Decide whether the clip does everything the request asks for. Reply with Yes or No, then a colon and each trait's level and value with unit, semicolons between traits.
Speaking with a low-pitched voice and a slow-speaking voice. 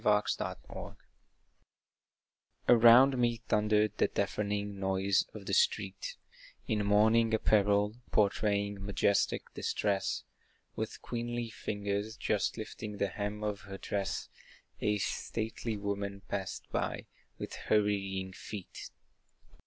Yes: low, 105 Hz; slow, 115 wpm